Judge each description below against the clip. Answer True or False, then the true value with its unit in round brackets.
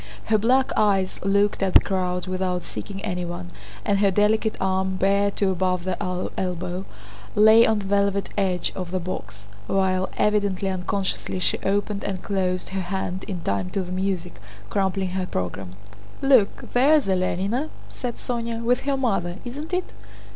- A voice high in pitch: True (195 Hz)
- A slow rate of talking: False (160 wpm)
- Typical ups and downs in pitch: False (2.3 semitones)